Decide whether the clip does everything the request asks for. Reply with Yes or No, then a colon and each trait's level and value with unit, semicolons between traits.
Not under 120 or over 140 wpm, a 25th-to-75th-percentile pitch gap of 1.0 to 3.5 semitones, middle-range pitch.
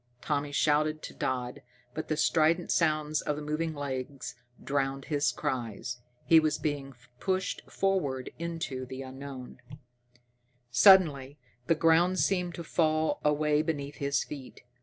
Yes: slow, 135 wpm; average, 2.9 semitones; medium, 150 Hz